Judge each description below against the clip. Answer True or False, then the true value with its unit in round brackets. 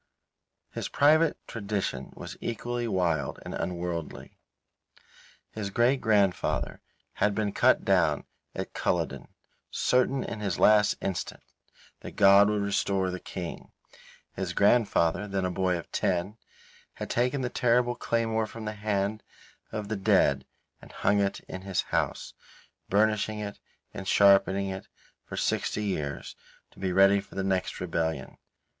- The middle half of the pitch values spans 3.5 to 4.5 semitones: False (2.6 semitones)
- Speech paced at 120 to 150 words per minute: True (140 wpm)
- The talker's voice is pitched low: True (100 Hz)